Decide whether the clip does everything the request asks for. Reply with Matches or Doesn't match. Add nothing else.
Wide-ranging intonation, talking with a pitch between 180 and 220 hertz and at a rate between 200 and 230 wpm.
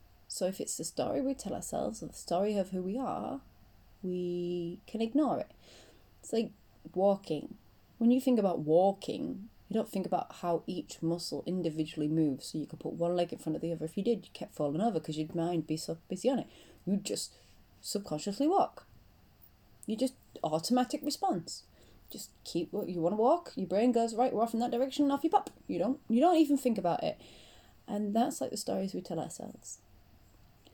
Matches